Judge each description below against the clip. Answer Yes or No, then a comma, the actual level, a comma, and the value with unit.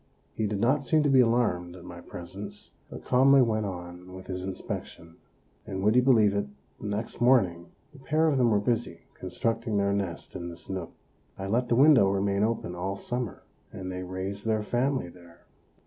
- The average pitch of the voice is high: No, low, 100 Hz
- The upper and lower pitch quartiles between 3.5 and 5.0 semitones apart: Yes, average, 4.7 semitones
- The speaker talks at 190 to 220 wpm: Yes, average, 195 wpm